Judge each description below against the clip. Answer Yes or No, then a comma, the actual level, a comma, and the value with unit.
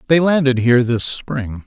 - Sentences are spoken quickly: No, average, 180 wpm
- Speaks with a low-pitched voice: Yes, low, 130 Hz